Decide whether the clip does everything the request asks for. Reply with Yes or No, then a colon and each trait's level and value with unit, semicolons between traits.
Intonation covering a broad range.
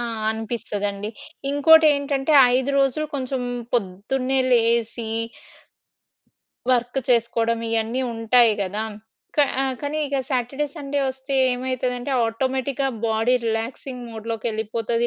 No: average, 3.0 semitones